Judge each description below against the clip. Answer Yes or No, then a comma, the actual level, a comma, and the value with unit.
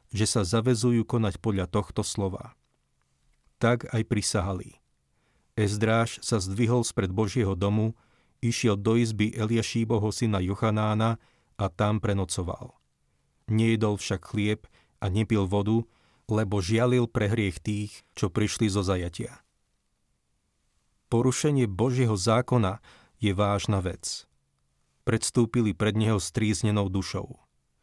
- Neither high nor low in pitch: No, low, 110 Hz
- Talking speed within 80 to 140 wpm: Yes, slow, 110 wpm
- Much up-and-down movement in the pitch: No, narrow, 2.4 semitones